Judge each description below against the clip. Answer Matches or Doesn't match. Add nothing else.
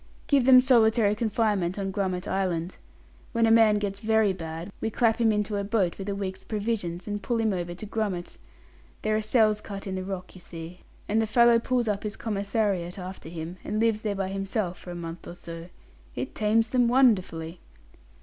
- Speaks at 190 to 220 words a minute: Matches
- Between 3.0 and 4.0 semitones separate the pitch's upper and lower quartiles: Matches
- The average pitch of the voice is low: Doesn't match